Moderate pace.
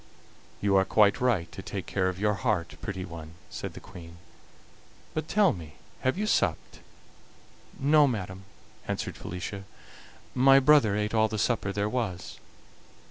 Yes: average, 150 wpm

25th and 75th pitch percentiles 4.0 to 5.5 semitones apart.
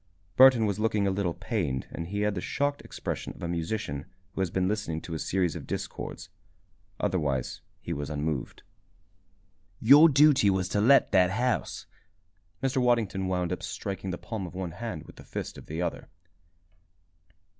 Yes: average, 4.5 semitones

